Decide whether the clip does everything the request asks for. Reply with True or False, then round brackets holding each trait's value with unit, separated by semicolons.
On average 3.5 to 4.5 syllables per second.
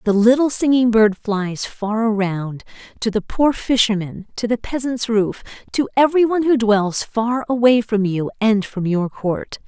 True (4.4 syllables/s)